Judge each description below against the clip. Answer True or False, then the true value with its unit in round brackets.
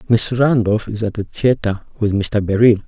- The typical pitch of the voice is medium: False (110 Hz)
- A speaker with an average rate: True (190 wpm)